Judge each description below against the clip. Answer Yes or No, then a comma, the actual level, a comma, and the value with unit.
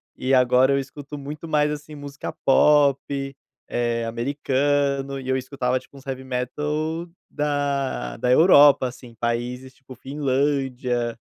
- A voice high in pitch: No, low, 135 Hz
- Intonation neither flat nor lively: No, narrow, 2.2 semitones